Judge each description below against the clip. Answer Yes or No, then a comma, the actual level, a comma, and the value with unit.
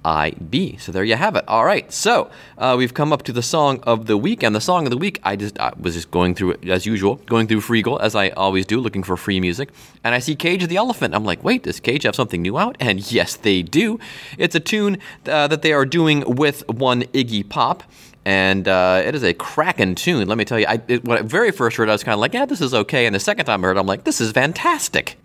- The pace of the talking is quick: Yes, fast, 275 wpm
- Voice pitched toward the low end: Yes, low, 115 Hz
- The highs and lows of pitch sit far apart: Yes, wide, 6.9 semitones